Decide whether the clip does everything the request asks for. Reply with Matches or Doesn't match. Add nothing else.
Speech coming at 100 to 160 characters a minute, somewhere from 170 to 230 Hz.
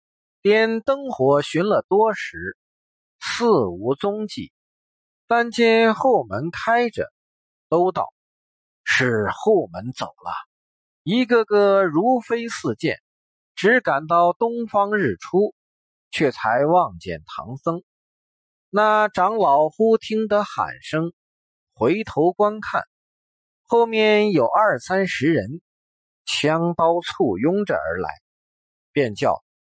Matches